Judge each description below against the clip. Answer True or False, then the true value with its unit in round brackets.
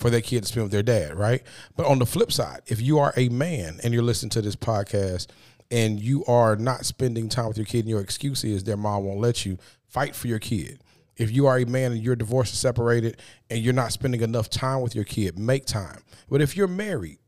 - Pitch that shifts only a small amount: False (3.1 semitones)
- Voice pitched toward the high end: False (120 Hz)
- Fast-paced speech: True (250 wpm)